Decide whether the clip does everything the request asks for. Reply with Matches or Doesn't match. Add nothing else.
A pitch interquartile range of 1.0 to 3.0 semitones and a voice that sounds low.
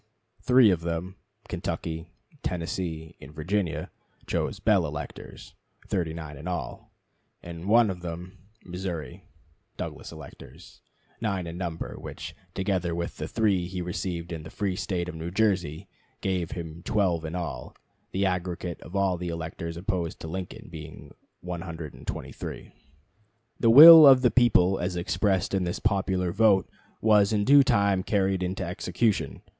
Matches